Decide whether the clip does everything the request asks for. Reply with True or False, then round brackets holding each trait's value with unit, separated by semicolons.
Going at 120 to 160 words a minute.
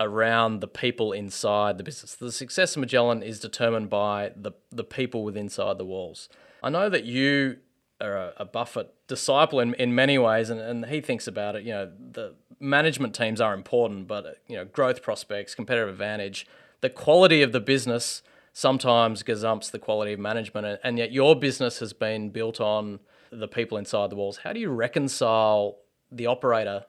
False (185 wpm)